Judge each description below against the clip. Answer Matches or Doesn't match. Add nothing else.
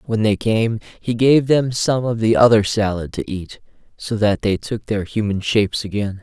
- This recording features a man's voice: Matches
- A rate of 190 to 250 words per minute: Matches